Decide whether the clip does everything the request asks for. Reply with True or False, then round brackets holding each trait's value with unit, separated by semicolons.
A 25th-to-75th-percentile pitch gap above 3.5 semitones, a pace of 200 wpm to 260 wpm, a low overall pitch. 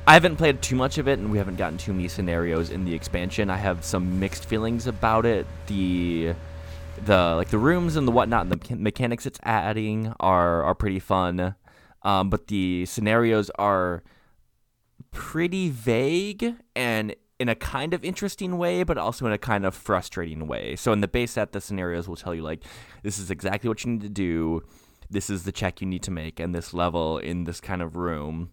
True (4.9 semitones; 205 wpm; 100 Hz)